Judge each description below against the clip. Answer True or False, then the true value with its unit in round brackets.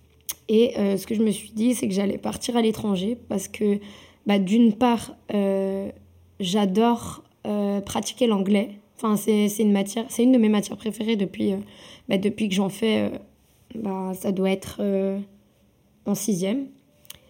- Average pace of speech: True (175 wpm)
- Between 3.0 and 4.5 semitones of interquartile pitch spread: False (2.4 semitones)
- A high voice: True (205 Hz)